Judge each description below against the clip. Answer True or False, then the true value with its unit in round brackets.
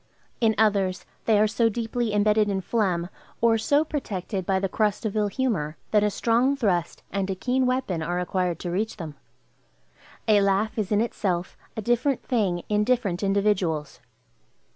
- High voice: True (210 Hz)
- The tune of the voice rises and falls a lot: False (3.4 semitones)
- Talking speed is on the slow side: False (170 wpm)